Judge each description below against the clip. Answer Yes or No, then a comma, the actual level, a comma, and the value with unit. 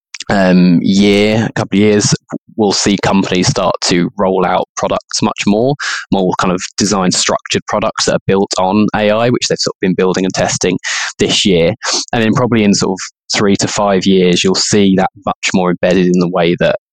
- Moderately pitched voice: No, very low, 95 Hz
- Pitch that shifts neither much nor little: No, narrow, 2.3 semitones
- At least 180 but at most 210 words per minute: Yes, average, 200 wpm